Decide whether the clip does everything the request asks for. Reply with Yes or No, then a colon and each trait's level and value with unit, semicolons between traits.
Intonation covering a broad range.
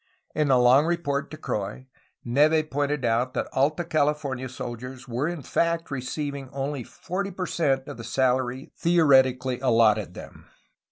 No: average, 3.3 semitones